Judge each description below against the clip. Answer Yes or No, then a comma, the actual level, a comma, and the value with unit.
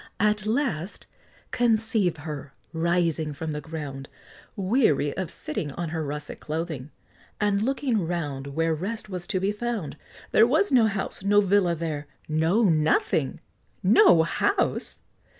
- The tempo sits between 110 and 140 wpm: Yes, slow, 135 wpm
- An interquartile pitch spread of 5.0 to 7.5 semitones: Yes, wide, 5.6 semitones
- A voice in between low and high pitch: Yes, medium, 175 Hz